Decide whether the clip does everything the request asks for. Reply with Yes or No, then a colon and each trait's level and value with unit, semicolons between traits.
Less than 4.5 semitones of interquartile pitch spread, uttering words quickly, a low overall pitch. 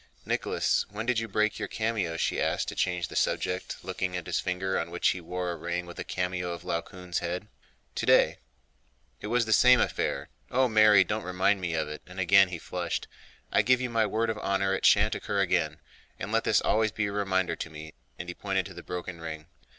Yes: average, 3.5 semitones; fast, 220 wpm; very low, 95 Hz